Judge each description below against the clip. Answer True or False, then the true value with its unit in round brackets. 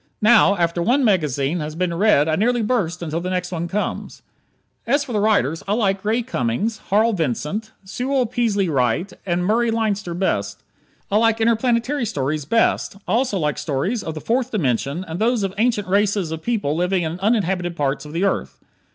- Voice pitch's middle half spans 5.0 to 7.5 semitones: True (5.5 semitones)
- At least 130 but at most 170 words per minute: False (185 wpm)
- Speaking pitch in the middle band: False (195 Hz)